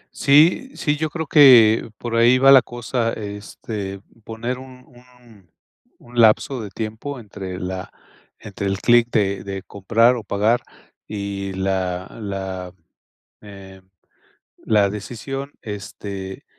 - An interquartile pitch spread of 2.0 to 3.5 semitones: No, average, 3.9 semitones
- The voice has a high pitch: No, low, 110 Hz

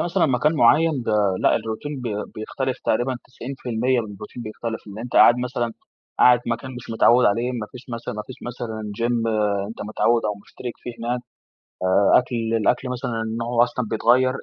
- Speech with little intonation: Yes, narrow, 2.0 semitones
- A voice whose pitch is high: No, low, 120 Hz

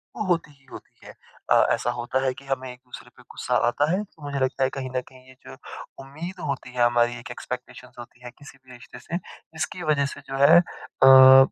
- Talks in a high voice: No, low, 135 Hz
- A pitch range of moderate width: No, narrow, 2.3 semitones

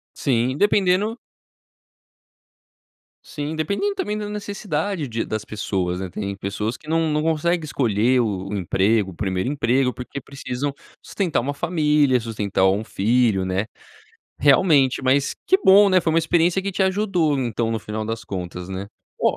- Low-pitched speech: Yes, low, 130 Hz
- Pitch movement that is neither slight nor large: No, wide, 7.7 semitones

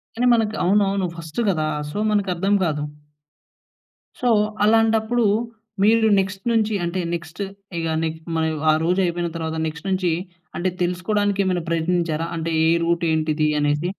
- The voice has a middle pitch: Yes, medium, 180 Hz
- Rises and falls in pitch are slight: No, average, 4.0 semitones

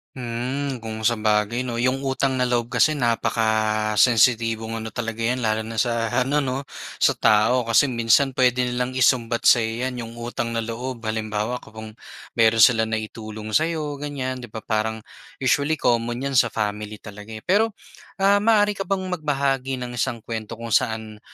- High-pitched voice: No, low, 120 Hz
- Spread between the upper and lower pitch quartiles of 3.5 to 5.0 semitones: No, average, 2.8 semitones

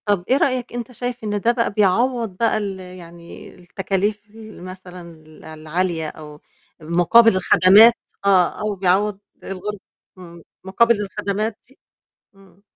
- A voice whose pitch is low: No, high, 195 Hz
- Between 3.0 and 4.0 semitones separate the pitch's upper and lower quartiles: Yes, average, 3.3 semitones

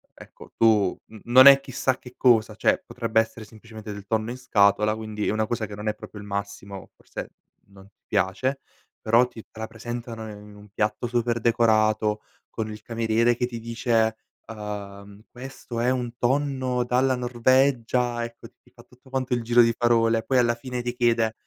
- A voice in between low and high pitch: No, low, 115 Hz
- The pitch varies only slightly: Yes, narrow, 2.3 semitones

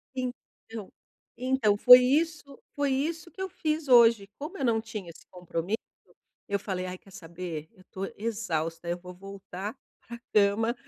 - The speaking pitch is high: Yes, high, 220 Hz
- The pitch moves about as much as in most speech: No, wide, 5.8 semitones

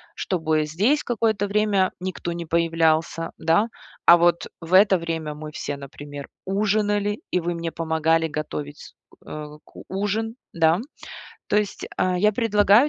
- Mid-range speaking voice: Yes, medium, 175 Hz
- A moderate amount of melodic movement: Yes, average, 4.2 semitones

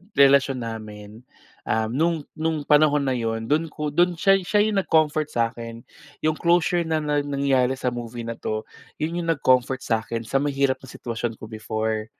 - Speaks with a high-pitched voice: No, low, 135 Hz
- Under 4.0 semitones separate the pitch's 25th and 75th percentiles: No, average, 5.2 semitones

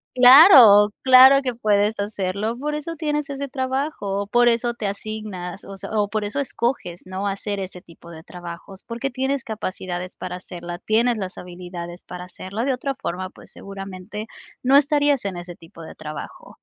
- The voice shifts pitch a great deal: Yes, wide, 5.8 semitones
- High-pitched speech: Yes, high, 210 Hz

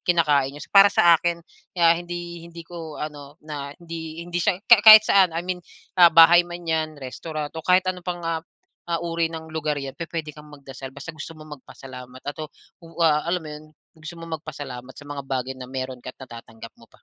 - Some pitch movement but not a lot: Yes, average, 3.2 semitones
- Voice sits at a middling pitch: Yes, medium, 160 Hz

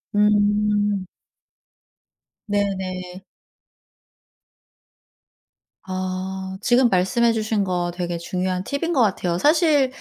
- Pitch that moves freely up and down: No, average, 2.7 semitones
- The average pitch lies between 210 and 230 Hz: No, high, 195 Hz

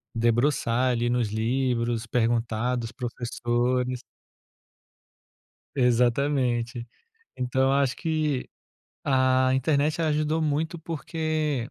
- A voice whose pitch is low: Yes, low, 125 Hz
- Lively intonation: No, average, 3.3 semitones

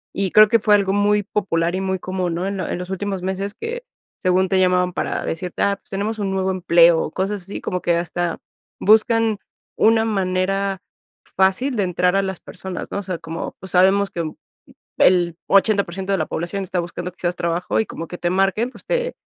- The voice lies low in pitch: No, high, 190 Hz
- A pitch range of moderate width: No, narrow, 2.1 semitones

